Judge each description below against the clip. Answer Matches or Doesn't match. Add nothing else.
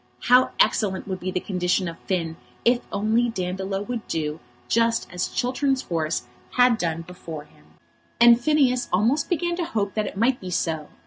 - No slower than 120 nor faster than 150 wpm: Doesn't match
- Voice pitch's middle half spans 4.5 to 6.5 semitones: Matches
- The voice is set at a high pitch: Matches